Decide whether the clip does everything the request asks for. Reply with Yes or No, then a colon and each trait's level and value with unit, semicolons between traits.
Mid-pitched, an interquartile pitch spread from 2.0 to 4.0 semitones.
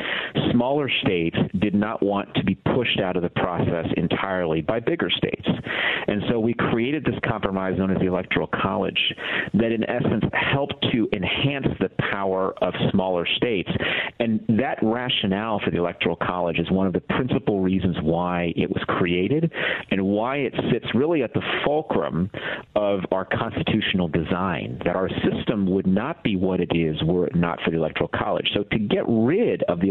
No: very low, 95 Hz; average, 2.9 semitones